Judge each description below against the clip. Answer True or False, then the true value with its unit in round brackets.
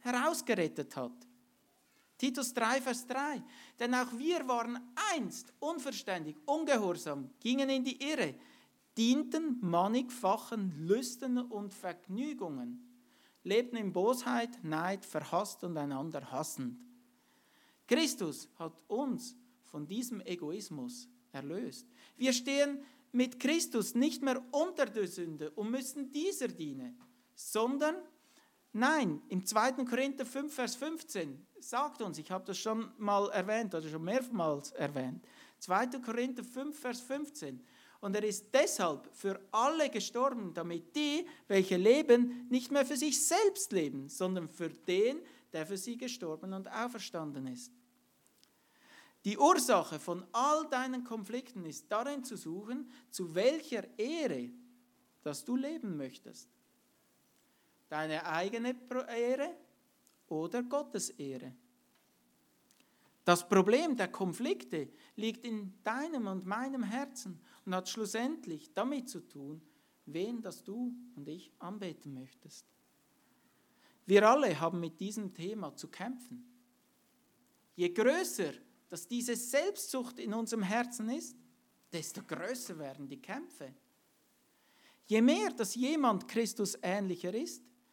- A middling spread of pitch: False (6.1 semitones)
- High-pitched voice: True (240 Hz)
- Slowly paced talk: True (120 wpm)